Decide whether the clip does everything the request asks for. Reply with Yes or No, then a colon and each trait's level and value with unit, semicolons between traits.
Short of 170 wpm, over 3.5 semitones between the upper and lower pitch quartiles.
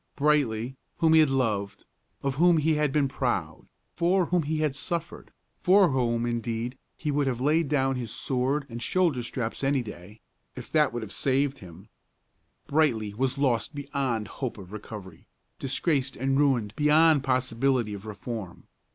Yes: average, 160 wpm; average, 4.5 semitones